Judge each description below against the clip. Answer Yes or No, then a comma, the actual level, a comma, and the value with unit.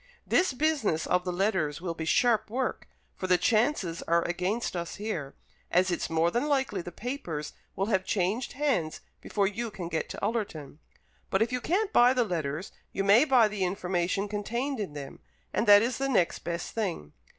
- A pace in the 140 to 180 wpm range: No, average, 190 wpm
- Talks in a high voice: Yes, high, 200 Hz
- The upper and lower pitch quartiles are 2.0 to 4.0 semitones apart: No, wide, 5.6 semitones